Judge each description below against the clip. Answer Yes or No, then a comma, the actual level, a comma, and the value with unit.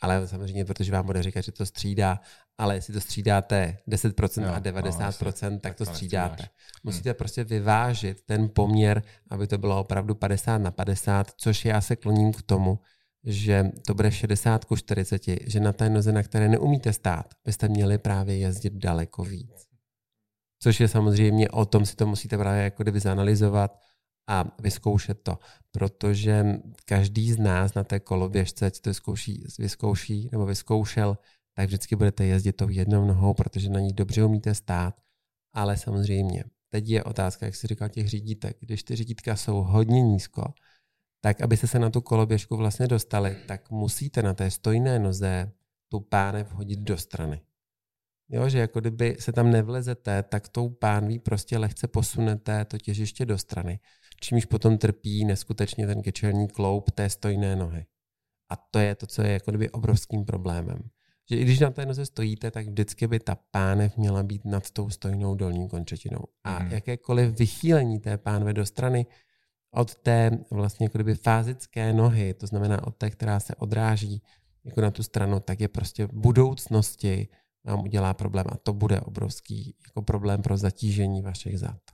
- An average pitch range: No, narrow, 2.1 semitones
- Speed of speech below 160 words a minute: No, fast, 170 wpm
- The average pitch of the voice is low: Yes, low, 105 Hz